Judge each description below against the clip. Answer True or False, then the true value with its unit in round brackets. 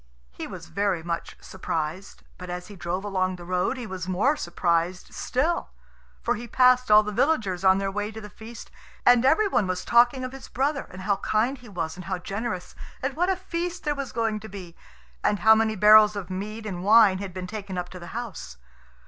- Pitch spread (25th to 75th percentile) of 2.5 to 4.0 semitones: False (4.7 semitones)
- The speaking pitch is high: True (210 Hz)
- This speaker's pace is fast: True (215 wpm)